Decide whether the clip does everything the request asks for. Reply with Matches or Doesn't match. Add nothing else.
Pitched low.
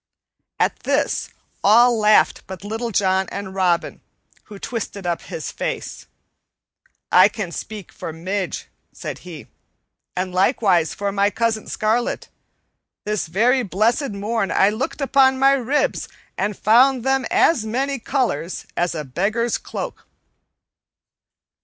Doesn't match